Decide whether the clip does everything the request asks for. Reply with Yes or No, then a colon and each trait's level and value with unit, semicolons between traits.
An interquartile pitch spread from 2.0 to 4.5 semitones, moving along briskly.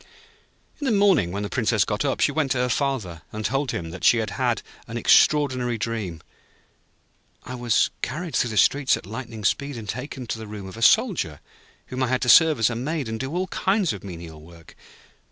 No: average, 5.3 semitones; fast, 215 wpm